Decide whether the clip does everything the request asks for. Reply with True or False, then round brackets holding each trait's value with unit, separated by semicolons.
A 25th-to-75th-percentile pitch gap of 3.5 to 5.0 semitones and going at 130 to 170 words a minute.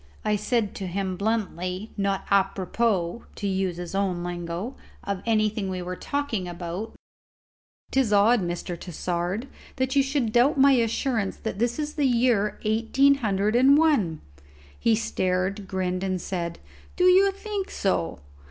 True (4.7 semitones; 145 wpm)